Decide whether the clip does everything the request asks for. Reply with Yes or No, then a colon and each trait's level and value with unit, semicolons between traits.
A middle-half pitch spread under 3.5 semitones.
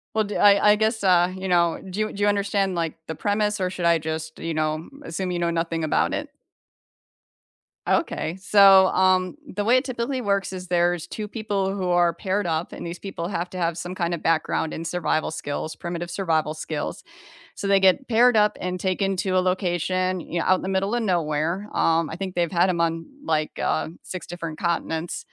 Yes: average, 2.8 semitones